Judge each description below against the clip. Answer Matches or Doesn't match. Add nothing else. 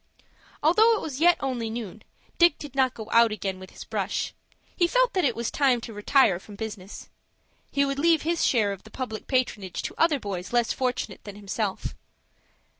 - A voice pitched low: Doesn't match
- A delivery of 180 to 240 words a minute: Matches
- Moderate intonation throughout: Doesn't match